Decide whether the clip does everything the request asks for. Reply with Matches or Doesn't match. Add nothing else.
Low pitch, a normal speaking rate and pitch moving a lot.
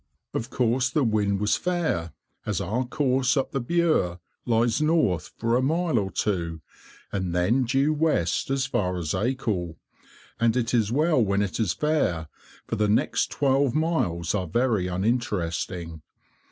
Matches